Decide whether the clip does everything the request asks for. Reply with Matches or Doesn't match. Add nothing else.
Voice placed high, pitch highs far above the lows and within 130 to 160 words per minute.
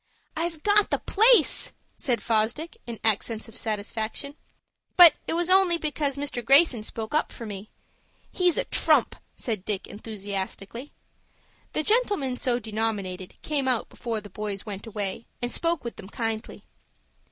Matches